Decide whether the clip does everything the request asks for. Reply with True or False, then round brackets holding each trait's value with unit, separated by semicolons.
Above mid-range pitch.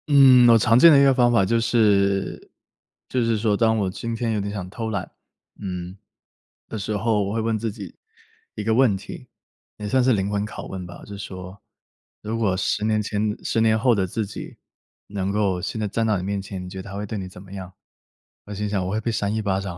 False (105 Hz)